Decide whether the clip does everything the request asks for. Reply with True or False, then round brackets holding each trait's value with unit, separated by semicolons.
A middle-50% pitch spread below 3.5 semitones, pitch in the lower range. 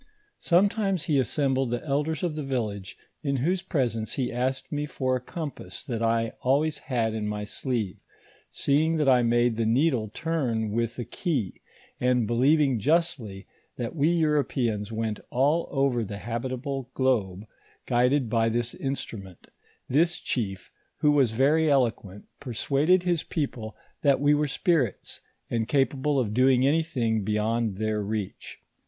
False (4.6 semitones; 130 Hz)